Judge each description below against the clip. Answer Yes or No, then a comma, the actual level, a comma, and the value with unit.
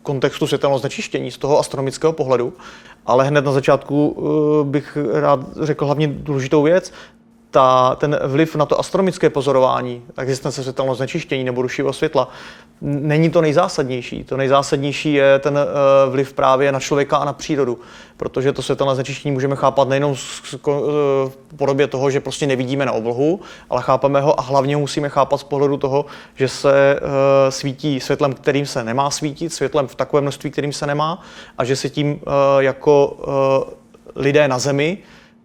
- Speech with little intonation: Yes, narrow, 1.6 semitones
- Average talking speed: Yes, average, 155 wpm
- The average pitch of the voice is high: No, medium, 140 Hz